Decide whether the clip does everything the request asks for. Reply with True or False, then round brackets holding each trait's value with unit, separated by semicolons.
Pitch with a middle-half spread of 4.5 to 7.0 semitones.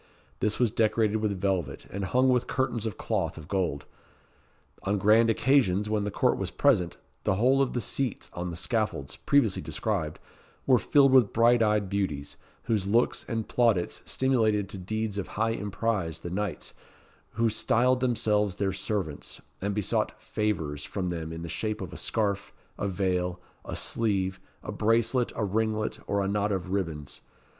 False (3.3 semitones)